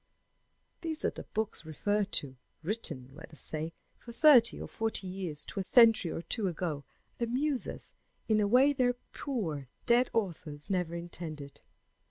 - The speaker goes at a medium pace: Yes, average, 155 wpm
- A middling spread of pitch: No, wide, 6.8 semitones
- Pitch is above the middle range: Yes, high, 195 Hz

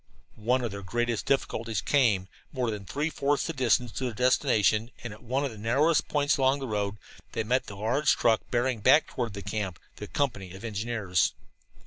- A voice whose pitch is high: No, low, 120 Hz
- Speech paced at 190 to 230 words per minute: Yes, average, 195 wpm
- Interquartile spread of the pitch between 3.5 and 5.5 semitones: Yes, average, 3.9 semitones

